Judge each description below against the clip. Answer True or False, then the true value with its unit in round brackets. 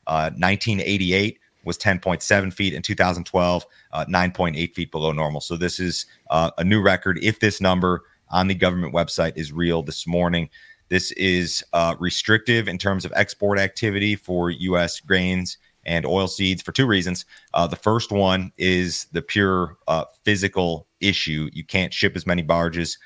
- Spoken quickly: False (175 wpm)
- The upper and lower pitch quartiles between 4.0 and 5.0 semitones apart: False (2.4 semitones)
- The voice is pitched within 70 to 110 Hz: True (90 Hz)